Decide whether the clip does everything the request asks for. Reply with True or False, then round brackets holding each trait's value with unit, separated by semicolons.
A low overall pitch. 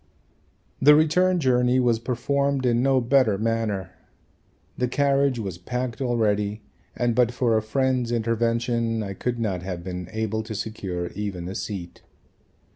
True (115 Hz)